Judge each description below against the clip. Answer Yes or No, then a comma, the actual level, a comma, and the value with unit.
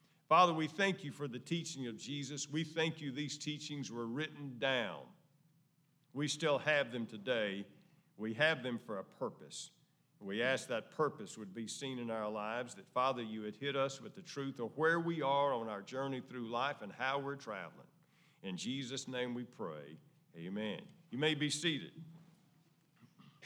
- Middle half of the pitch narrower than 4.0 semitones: No, average, 4.7 semitones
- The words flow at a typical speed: Yes, average, 180 wpm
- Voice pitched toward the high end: No, medium, 140 Hz